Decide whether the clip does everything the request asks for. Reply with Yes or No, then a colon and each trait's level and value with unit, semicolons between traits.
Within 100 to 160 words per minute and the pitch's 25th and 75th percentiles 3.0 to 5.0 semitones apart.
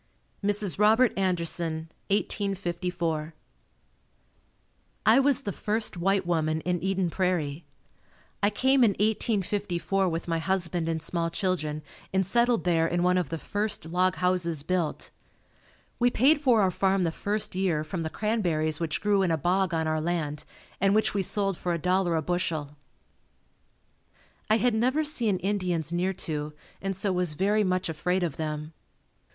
Yes: average, 155 wpm; average, 3.6 semitones